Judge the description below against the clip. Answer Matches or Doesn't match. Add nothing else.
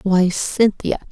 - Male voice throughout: Doesn't match